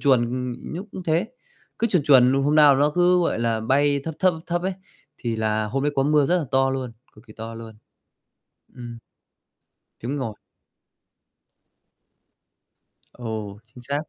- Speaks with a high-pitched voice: No, low, 135 Hz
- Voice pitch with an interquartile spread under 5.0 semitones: Yes, average, 4.6 semitones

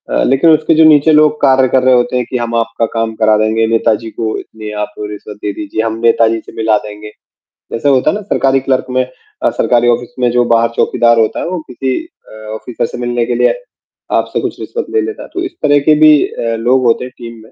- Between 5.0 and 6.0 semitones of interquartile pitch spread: No, average, 3.1 semitones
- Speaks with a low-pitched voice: Yes, low, 120 Hz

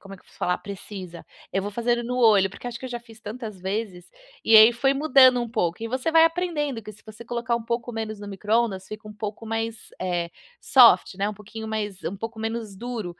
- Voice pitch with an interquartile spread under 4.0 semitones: Yes, average, 2.8 semitones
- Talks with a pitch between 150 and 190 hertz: No, high, 225 Hz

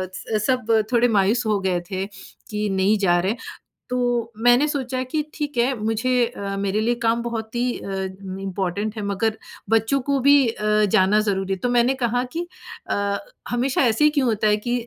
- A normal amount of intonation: Yes, average, 3.7 semitones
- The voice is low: No, high, 220 Hz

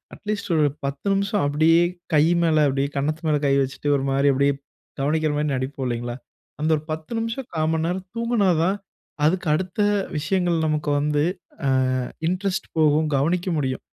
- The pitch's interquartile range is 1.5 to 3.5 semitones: No, average, 4.3 semitones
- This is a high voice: No, medium, 155 Hz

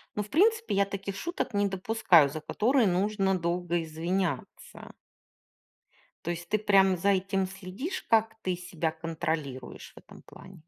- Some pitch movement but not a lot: Yes, average, 3.2 semitones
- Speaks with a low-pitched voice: No, high, 190 Hz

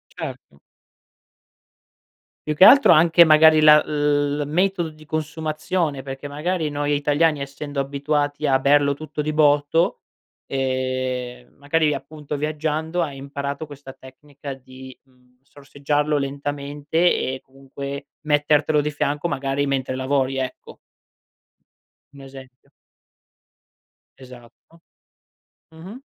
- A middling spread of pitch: No, narrow, 2.1 semitones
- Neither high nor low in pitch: Yes, medium, 145 Hz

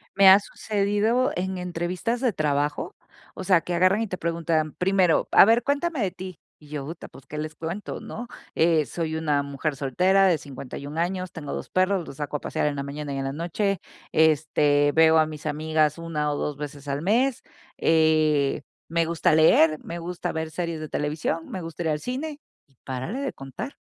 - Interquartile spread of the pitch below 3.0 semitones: No, average, 3.9 semitones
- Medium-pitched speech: Yes, medium, 160 Hz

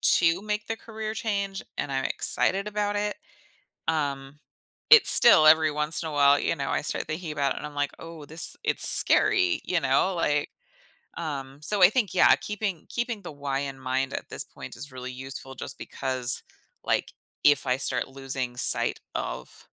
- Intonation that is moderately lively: No, wide, 6.7 semitones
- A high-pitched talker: No, medium, 150 Hz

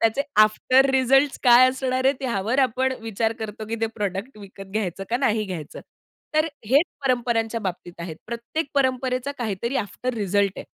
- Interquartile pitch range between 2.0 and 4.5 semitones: Yes, average, 3.9 semitones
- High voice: Yes, high, 235 Hz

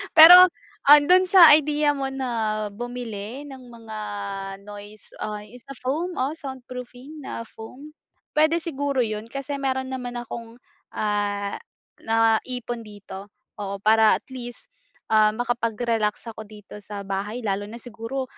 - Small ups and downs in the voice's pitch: No, average, 4.2 semitones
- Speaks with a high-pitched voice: Yes, high, 240 Hz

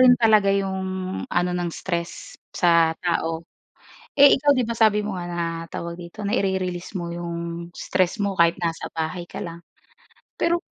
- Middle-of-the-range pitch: Yes, medium, 180 Hz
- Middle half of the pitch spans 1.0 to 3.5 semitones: Yes, average, 3.1 semitones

